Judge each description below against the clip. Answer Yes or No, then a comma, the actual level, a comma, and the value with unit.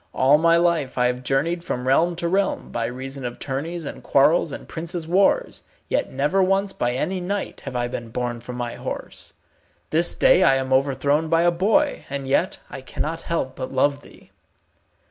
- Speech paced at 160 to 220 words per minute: Yes, average, 190 wpm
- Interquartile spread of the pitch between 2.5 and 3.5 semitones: No, average, 4.7 semitones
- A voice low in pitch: No, medium, 145 Hz